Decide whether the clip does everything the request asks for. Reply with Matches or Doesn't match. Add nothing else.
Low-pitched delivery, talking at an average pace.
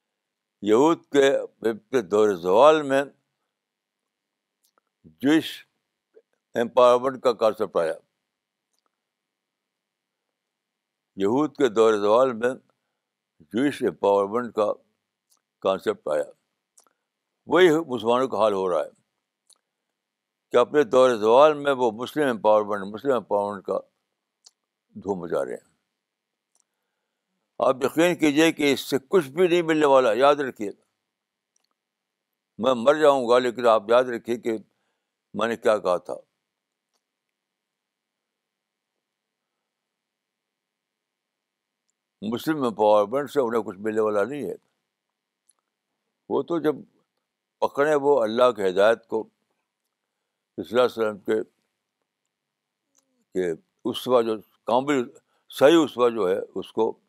Doesn't match